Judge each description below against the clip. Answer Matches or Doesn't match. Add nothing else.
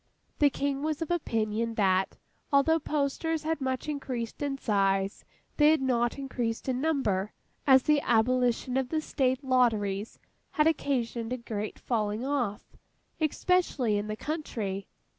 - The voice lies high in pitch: Matches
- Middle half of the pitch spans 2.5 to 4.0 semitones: Doesn't match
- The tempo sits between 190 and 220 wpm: Doesn't match